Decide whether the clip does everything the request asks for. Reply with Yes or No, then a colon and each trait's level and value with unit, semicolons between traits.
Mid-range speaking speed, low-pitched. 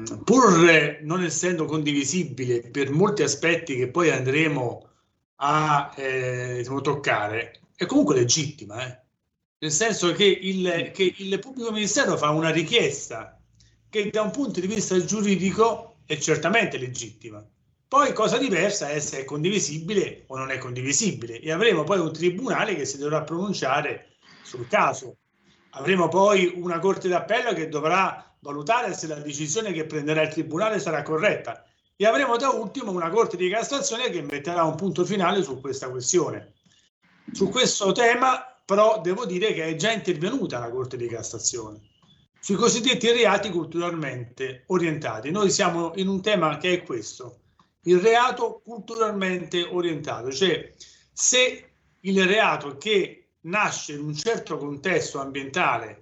No: average, 145 wpm; medium, 170 Hz